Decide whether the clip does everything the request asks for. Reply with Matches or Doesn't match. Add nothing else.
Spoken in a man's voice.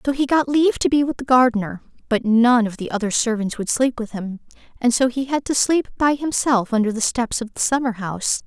Doesn't match